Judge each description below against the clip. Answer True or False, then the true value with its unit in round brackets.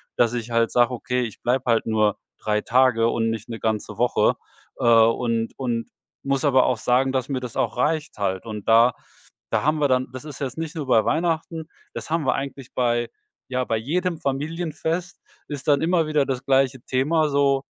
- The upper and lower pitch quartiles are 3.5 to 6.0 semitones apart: True (4.1 semitones)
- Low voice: True (130 Hz)